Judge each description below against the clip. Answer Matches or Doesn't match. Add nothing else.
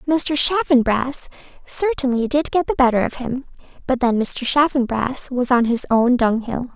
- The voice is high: Matches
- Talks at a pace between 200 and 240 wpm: Doesn't match